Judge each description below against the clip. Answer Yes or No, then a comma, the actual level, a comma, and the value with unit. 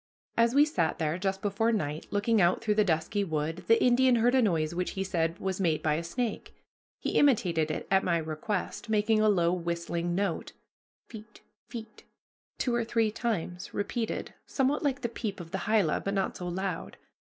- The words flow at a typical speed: Yes, average, 190 wpm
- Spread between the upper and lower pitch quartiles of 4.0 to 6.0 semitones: Yes, average, 4.9 semitones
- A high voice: Yes, high, 195 Hz